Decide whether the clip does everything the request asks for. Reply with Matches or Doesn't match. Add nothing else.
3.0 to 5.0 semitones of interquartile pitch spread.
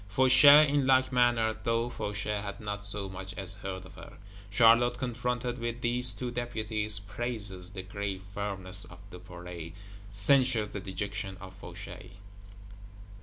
Matches